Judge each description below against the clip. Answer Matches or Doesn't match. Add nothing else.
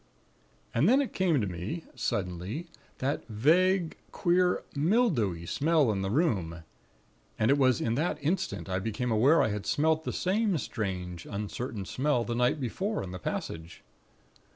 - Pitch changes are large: Matches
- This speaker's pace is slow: Doesn't match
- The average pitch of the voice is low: Matches